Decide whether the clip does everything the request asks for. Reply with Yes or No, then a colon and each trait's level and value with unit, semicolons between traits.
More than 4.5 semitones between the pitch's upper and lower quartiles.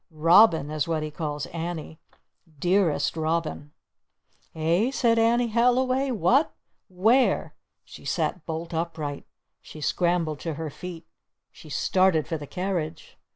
No: average, 4.2 semitones